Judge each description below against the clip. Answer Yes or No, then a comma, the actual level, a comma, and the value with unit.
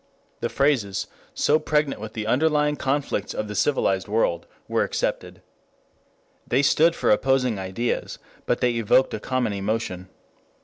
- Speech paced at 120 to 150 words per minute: Yes, average, 140 wpm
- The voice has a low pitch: Yes, low, 120 Hz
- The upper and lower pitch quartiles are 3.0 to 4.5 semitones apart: No, average, 5.1 semitones